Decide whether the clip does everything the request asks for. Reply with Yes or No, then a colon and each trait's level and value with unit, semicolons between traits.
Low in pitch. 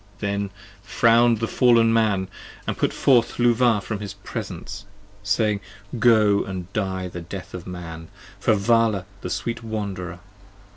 Yes: low, 105 Hz